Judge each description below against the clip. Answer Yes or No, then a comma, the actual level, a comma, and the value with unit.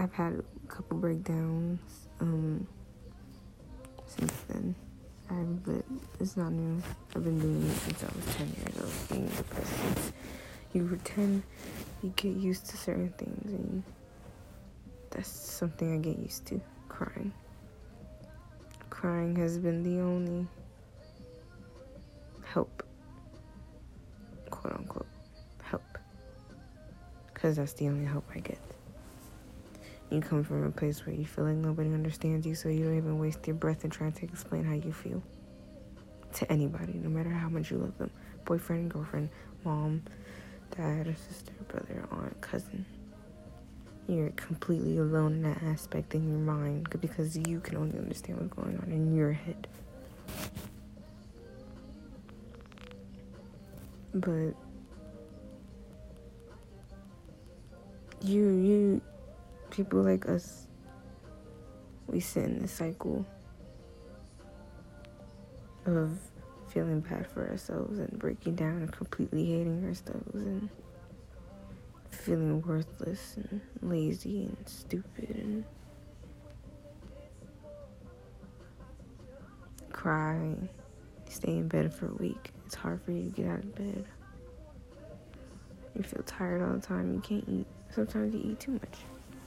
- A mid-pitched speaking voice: Yes, medium, 155 Hz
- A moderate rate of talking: No, slow, 120 wpm